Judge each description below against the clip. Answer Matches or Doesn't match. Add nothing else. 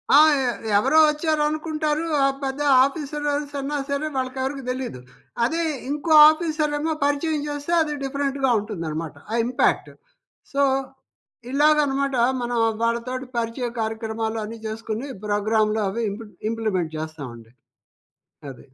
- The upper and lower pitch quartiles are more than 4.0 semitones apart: Matches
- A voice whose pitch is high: Matches